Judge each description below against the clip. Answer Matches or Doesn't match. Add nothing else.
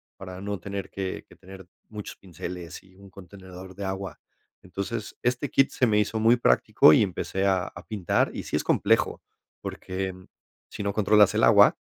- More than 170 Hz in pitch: Doesn't match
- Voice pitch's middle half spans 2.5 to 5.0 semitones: Doesn't match